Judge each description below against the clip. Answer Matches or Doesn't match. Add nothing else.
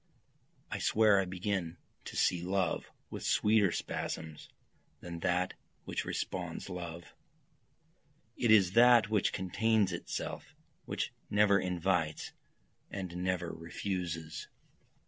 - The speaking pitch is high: Doesn't match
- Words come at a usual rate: Doesn't match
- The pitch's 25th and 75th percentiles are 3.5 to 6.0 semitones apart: Doesn't match